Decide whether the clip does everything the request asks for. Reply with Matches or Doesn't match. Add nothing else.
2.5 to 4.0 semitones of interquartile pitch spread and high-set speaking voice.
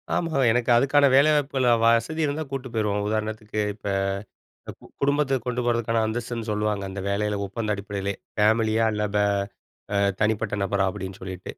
Doesn't match